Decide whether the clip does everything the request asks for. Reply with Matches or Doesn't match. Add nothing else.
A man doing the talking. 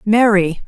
Doesn't match